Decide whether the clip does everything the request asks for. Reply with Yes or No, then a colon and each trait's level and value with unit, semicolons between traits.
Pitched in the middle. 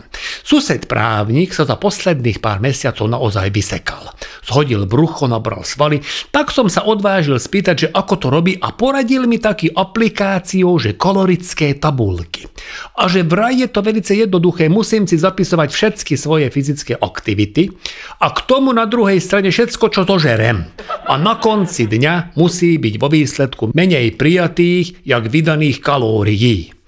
Yes: medium, 165 Hz